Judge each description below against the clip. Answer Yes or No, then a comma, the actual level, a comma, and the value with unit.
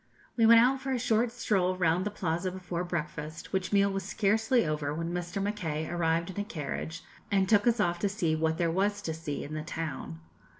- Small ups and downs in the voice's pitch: No, average, 4.1 semitones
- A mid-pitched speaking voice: Yes, medium, 180 Hz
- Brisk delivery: Yes, fast, 215 wpm